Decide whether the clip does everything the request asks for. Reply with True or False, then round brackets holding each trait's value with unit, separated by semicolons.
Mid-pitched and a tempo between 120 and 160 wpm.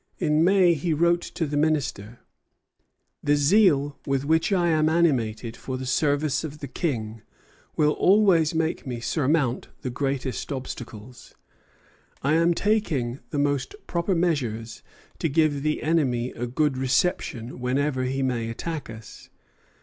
True (145 Hz; 140 wpm)